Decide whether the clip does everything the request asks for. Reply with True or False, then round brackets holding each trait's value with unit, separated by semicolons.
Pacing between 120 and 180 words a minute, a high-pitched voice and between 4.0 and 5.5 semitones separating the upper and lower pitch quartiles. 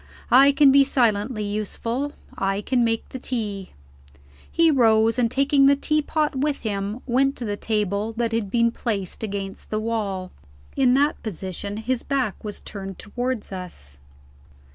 True (155 wpm; 230 Hz; 4.5 semitones)